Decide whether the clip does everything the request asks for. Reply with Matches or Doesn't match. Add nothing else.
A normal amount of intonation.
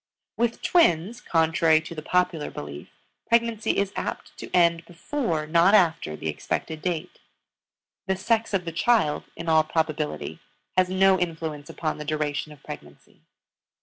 Matches